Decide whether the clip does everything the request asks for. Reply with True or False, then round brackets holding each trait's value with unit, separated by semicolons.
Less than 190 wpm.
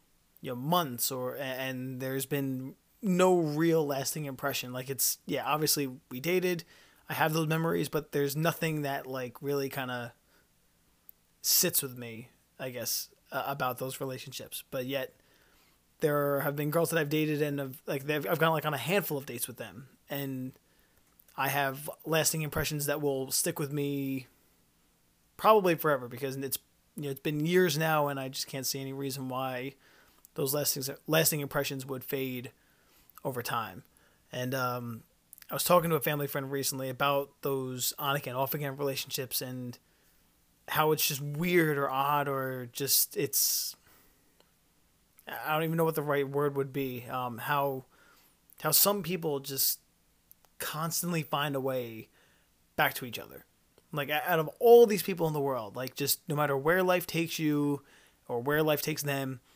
True (170 wpm)